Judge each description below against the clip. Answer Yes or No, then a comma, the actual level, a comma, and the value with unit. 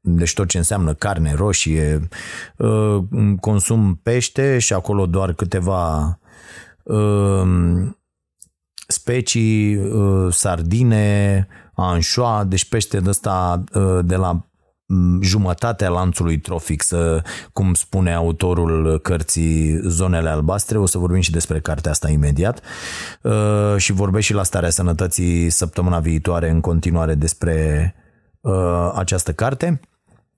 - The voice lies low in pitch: Yes, very low, 90 Hz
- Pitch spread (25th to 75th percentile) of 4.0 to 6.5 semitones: No, average, 3.5 semitones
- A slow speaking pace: Yes, slow, 100 wpm